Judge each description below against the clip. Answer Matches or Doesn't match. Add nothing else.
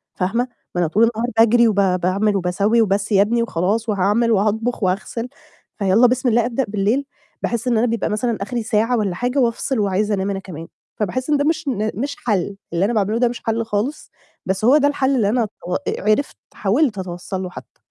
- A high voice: Matches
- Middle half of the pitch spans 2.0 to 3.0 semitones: Doesn't match